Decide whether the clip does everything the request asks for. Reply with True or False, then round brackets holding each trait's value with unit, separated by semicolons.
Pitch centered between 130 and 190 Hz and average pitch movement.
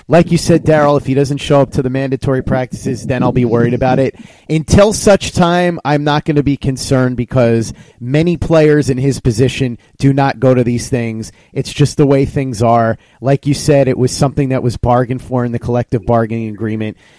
True (135 Hz; 3.0 semitones)